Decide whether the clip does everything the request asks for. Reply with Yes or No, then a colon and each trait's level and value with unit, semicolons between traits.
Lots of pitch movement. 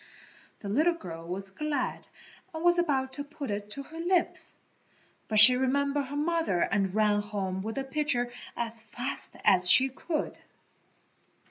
Yes: wide, 6.3 semitones